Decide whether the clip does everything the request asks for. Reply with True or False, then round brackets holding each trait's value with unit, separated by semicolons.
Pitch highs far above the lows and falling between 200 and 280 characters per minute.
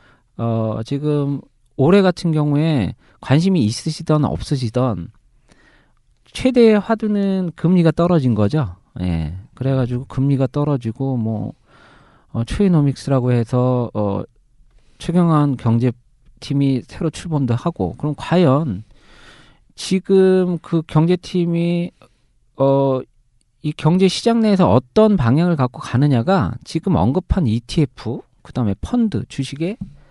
True (5.9 semitones; 245 characters per minute)